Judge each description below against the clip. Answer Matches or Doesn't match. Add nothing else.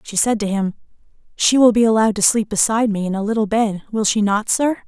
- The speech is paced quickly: Matches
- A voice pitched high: Matches